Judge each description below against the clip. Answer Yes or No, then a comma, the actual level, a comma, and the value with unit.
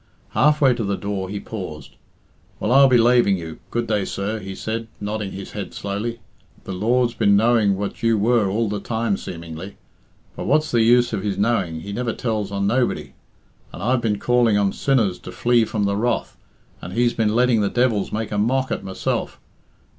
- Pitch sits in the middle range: No, low, 110 Hz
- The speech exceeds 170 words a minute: Yes, average, 200 wpm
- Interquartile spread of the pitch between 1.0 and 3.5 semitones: Yes, average, 3.1 semitones